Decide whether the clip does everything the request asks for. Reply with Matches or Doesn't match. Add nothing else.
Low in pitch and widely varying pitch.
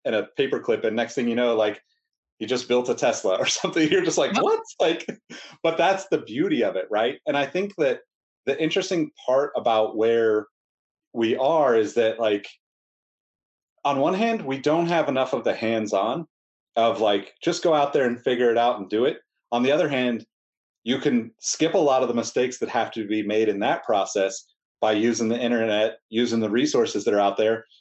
Matches